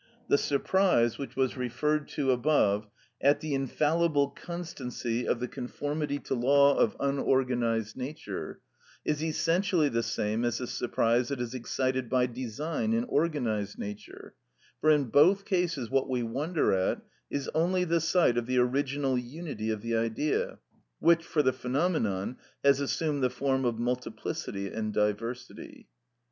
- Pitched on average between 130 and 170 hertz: Yes, low, 135 Hz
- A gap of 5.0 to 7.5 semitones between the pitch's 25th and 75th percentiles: No, average, 4.3 semitones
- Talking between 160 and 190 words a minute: No, average, 150 wpm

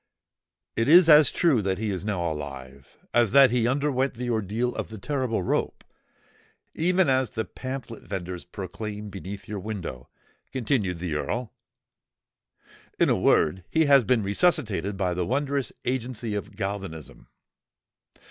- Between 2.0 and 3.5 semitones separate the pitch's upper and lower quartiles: No, wide, 5.6 semitones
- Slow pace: No, average, 145 wpm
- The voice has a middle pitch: No, low, 110 Hz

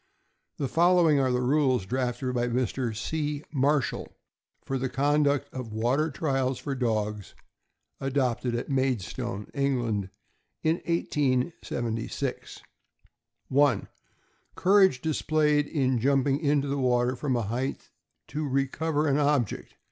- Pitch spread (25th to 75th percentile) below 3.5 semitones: Yes, average, 3.1 semitones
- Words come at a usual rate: No, slow, 120 wpm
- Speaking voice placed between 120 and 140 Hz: Yes, low, 135 Hz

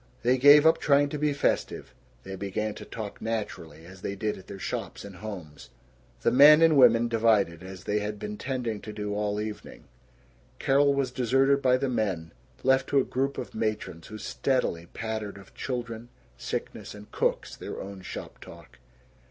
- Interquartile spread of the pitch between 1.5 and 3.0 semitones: No, average, 4.9 semitones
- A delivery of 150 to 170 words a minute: No, average, 180 wpm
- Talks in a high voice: No, low, 110 Hz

